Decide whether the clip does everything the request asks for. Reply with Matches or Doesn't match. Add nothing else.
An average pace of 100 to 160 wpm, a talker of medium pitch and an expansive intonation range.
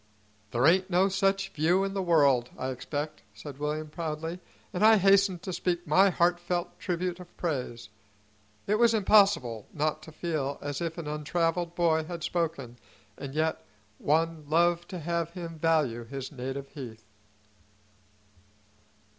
Doesn't match